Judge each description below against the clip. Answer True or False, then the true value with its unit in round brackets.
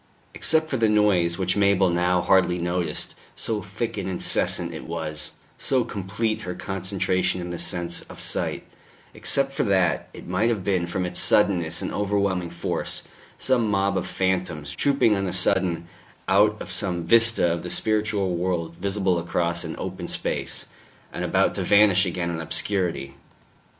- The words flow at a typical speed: True (165 wpm)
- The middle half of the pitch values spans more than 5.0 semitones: False (2.8 semitones)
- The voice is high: False (95 Hz)